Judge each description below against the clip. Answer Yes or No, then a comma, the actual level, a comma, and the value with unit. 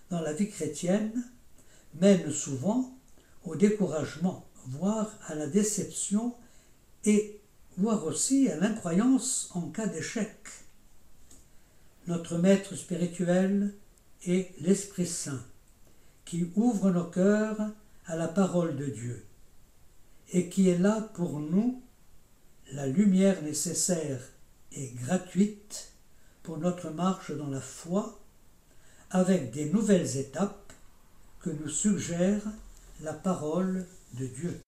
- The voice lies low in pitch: No, medium, 180 Hz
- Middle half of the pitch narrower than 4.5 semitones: No, average, 5.3 semitones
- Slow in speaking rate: Yes, slow, 105 wpm